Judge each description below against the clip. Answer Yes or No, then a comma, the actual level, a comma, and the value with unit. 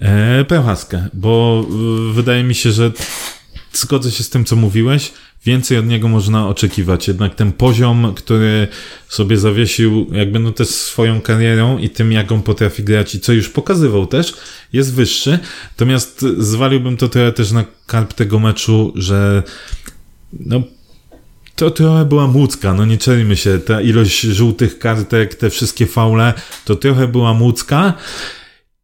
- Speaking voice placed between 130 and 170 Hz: No, low, 115 Hz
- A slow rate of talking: No, average, 150 wpm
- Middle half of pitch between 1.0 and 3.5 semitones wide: Yes, narrow, 2.4 semitones